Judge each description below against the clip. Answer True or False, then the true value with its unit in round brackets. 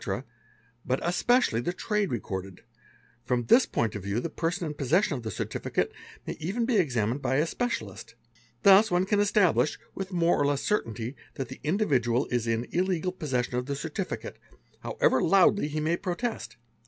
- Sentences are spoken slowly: False (175 wpm)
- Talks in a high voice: False (155 Hz)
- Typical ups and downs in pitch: False (7.7 semitones)